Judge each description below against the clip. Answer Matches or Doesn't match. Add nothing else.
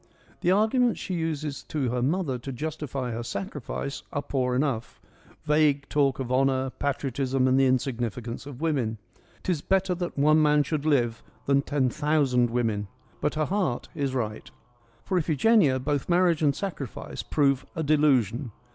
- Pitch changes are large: Doesn't match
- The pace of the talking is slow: Doesn't match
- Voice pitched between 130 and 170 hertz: Matches